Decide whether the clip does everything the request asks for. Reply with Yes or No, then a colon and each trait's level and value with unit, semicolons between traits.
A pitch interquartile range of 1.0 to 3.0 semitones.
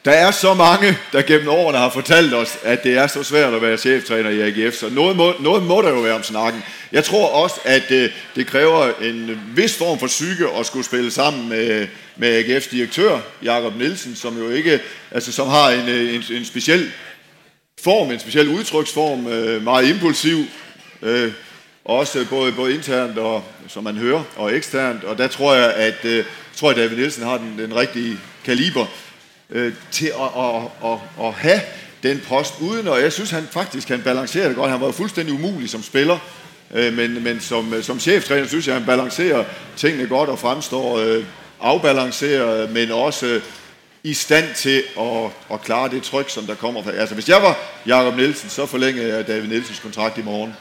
No: average, 3.7 semitones